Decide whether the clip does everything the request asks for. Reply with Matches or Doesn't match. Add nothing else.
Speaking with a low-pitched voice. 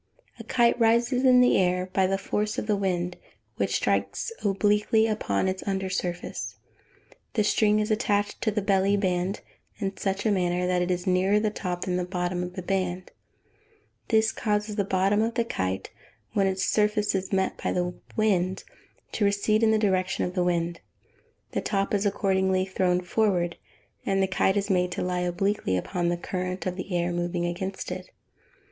Doesn't match